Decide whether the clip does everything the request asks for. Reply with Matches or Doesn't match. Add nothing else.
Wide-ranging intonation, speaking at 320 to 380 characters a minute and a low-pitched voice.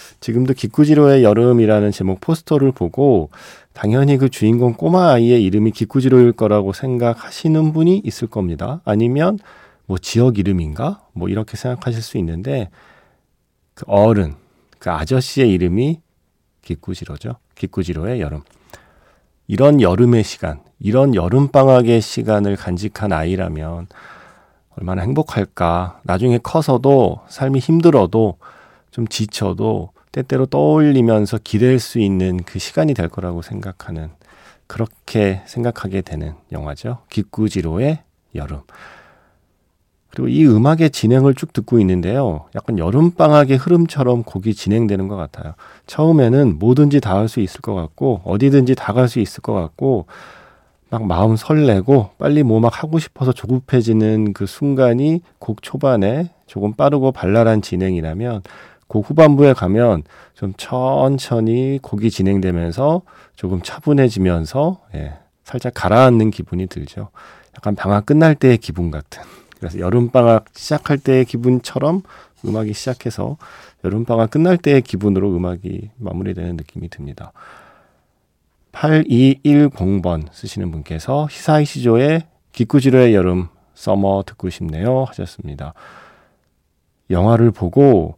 Doesn't match